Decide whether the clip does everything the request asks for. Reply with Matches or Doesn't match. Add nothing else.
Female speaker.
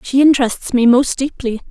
Matches